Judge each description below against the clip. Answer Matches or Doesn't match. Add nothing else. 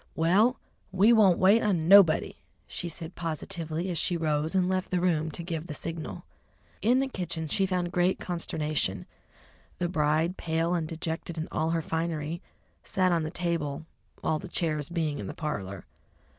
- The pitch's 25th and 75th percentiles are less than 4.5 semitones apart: Matches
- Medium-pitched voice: Matches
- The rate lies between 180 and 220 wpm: Doesn't match